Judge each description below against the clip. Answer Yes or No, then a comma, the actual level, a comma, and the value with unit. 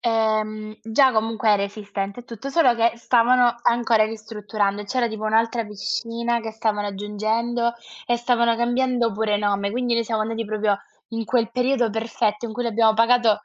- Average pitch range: No, narrow, 1.8 semitones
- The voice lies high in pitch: Yes, high, 225 Hz